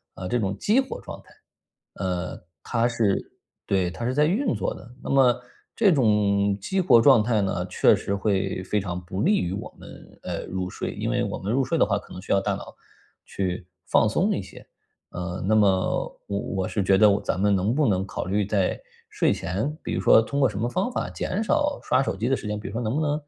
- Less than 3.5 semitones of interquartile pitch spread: No, wide, 5.5 semitones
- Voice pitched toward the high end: No, low, 105 Hz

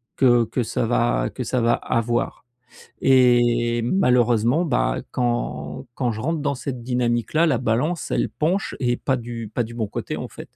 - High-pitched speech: No, low, 120 Hz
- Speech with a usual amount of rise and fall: No, narrow, 1.9 semitones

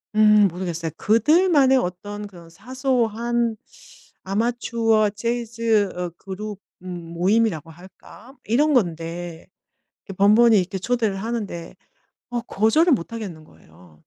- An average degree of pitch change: Yes, average, 4.8 semitones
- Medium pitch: No, high, 210 Hz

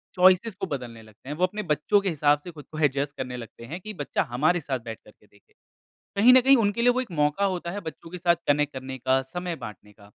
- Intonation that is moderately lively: No, wide, 5.9 semitones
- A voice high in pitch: No, medium, 150 Hz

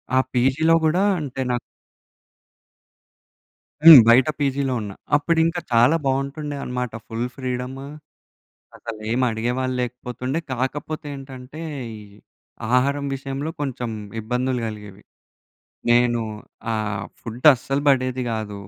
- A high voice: No, low, 130 Hz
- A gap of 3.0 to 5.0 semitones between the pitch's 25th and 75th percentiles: No, narrow, 2.6 semitones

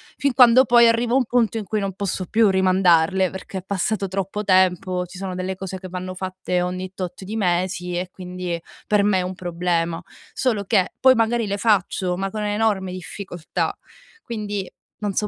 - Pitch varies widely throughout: No, narrow, 2.6 semitones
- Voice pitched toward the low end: No, high, 190 Hz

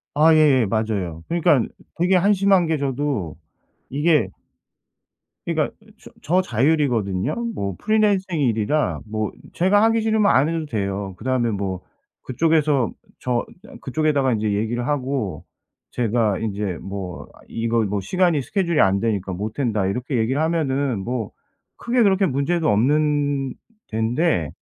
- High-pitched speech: No, low, 130 Hz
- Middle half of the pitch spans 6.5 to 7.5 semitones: Yes, wide, 7.0 semitones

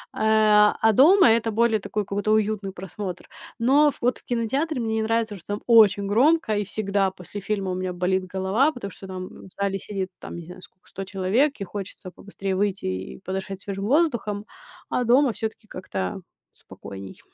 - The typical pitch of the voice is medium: No, high, 205 Hz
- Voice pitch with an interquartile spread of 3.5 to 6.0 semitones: No, average, 3.1 semitones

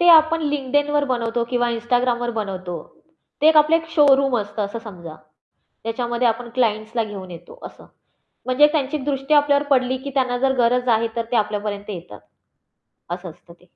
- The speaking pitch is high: Yes, high, 245 Hz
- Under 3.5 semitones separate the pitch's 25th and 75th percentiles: No, average, 4.6 semitones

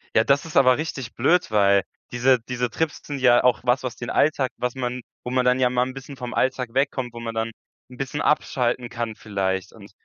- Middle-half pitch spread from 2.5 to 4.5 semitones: No, narrow, 2.1 semitones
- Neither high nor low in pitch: No, low, 125 Hz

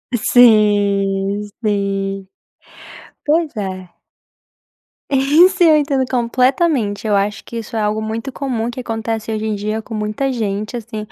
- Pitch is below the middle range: No, high, 220 Hz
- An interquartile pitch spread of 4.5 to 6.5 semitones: No, average, 3.7 semitones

